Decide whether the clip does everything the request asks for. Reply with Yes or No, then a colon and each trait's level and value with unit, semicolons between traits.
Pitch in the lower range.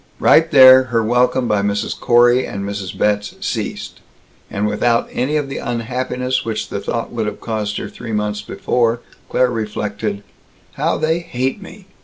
Yes: low, 115 Hz